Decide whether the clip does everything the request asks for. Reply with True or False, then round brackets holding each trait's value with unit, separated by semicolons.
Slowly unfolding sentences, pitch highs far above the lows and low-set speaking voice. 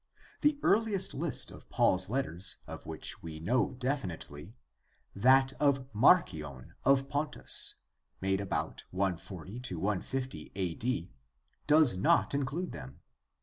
True (110 wpm; 7.4 semitones; 115 Hz)